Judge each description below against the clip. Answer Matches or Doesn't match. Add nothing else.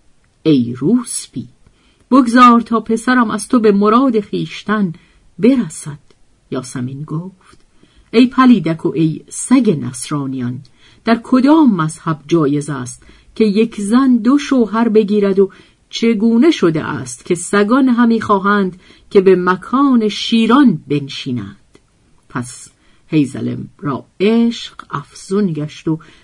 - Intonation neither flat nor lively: Doesn't match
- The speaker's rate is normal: Matches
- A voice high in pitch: Matches